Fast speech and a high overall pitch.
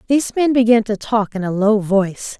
Yes: fast, 225 wpm; high, 220 Hz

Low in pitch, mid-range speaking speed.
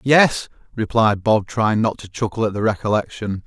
Yes: low, 110 Hz; average, 175 wpm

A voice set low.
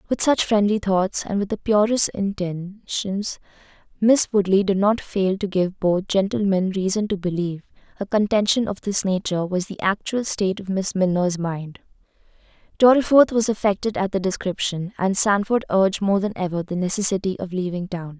No: high, 195 Hz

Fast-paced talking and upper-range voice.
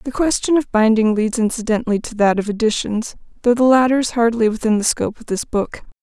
Yes: fast, 210 wpm; high, 230 Hz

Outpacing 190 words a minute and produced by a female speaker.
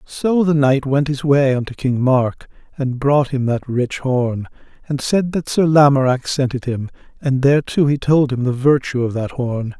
No: average, 200 wpm; male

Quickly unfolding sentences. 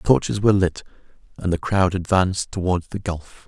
No: average, 190 wpm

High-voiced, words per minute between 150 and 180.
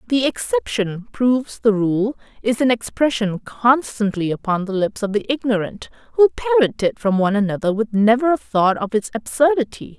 Yes: high, 230 Hz; average, 170 wpm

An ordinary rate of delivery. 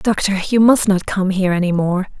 No: fast, 220 wpm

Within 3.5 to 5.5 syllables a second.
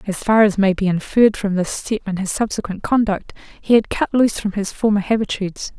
No: 5.8 syllables/s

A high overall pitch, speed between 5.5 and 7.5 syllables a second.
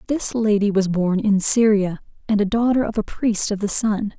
No: high, 210 Hz; 4.9 syllables/s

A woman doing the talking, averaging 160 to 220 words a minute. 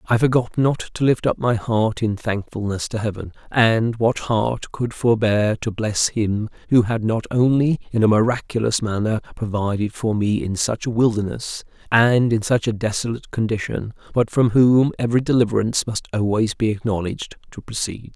No: male; average, 170 wpm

